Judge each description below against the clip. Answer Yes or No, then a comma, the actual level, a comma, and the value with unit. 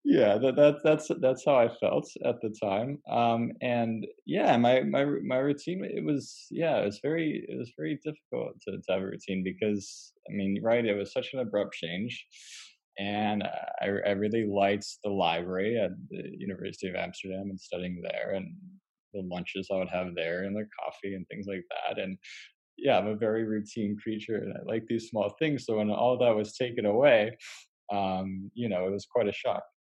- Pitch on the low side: Yes, low, 105 Hz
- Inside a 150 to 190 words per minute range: No, average, 200 wpm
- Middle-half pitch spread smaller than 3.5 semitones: No, average, 4.3 semitones